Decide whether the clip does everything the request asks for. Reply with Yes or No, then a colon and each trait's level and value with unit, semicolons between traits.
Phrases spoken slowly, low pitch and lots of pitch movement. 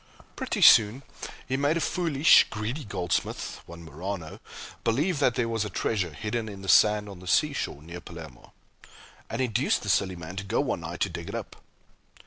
No: average, 190 wpm; low, 105 Hz; wide, 6.2 semitones